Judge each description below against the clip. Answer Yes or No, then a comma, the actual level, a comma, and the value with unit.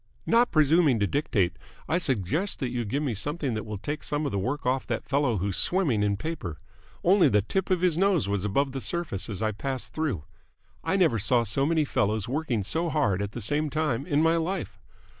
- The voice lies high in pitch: No, low, 135 Hz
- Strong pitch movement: Yes, wide, 7.0 semitones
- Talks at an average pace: No, fast, 215 wpm